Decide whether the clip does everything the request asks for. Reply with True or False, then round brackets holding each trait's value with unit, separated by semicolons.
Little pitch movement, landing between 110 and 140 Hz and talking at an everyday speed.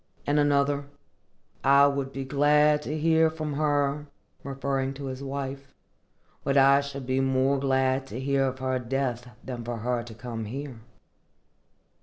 True (1.4 semitones; 135 Hz; 145 wpm)